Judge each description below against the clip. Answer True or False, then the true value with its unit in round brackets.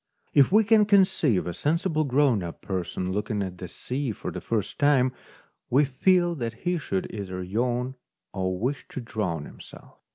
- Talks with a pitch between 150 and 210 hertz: False (125 Hz)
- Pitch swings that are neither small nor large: False (7.6 semitones)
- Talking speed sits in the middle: True (170 wpm)